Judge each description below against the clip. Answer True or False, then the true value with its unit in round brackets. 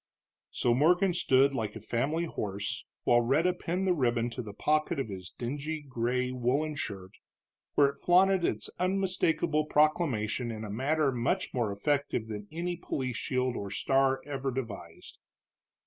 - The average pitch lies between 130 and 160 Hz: True (135 Hz)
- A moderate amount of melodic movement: True (5.0 semitones)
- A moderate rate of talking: True (155 wpm)